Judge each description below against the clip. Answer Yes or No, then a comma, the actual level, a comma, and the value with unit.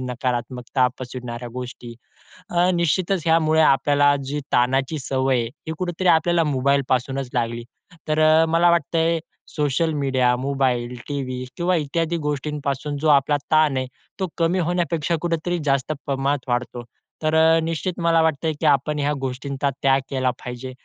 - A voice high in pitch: No, medium, 145 Hz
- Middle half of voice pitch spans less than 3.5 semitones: No, average, 3.8 semitones